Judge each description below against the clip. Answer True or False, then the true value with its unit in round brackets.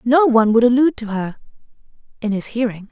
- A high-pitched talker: True (235 Hz)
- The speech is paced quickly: False (185 wpm)